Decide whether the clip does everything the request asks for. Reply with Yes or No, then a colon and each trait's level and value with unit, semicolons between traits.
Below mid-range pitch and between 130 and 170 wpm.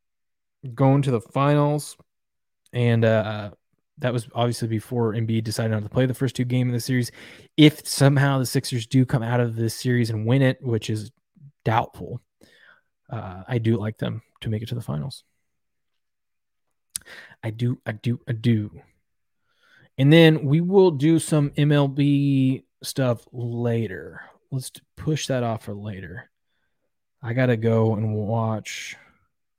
Yes: low, 120 Hz; average, 155 wpm